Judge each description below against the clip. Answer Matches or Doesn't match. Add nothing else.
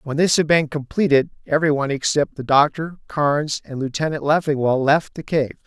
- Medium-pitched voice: Matches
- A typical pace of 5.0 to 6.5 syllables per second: Matches